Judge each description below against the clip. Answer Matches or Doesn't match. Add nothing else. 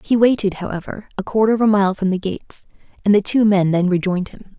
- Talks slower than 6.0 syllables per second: Doesn't match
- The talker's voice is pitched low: Doesn't match